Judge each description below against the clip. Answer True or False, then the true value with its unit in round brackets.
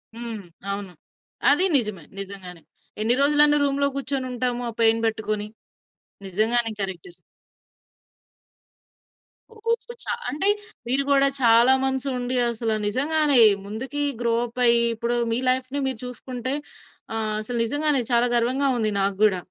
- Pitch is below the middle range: False (240 Hz)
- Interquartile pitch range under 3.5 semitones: False (3.9 semitones)